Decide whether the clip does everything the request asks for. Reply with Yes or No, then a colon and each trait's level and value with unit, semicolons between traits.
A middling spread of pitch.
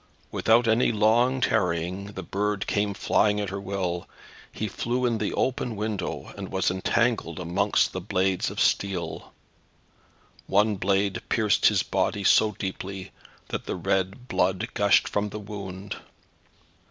No: narrow, 2.3 semitones